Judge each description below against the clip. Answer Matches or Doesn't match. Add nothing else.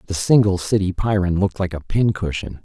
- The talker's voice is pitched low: Matches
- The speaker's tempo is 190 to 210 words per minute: Matches